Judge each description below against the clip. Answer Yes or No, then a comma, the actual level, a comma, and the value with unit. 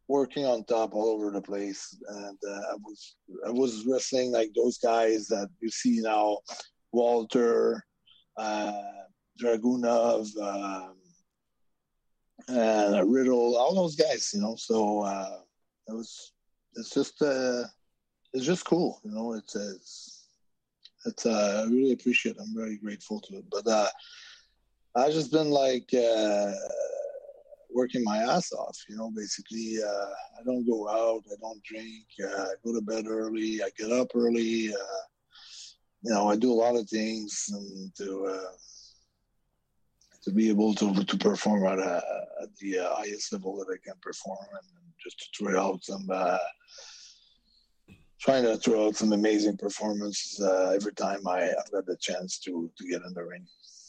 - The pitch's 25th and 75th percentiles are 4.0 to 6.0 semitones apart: No, average, 3.1 semitones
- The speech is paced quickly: No, average, 160 wpm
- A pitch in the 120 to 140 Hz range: No, low, 110 Hz